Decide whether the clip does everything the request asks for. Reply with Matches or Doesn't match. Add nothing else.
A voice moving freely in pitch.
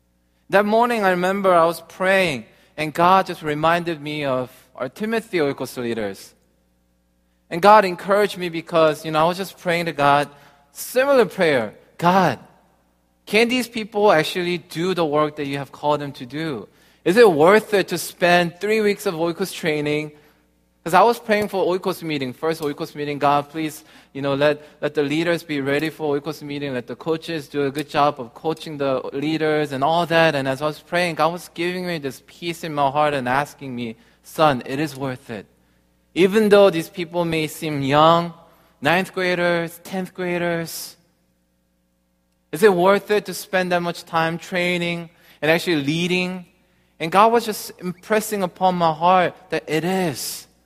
Doesn't match